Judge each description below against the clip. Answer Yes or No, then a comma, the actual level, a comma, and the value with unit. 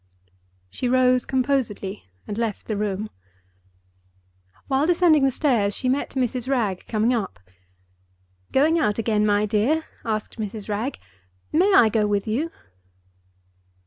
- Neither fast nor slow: No, slow, 130 wpm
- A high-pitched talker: Yes, high, 230 Hz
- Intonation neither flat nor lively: Yes, average, 4.2 semitones